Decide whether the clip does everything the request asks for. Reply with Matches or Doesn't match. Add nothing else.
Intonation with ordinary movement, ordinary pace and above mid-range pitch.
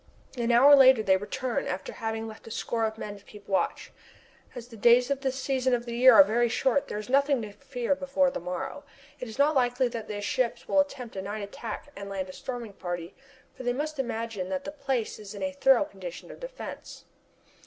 Doesn't match